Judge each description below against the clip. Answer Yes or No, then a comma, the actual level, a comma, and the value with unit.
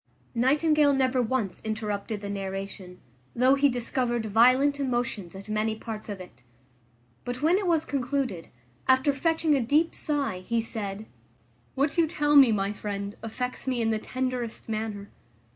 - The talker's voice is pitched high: Yes, high, 240 Hz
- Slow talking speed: No, average, 155 wpm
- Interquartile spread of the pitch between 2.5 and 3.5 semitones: No, average, 4.7 semitones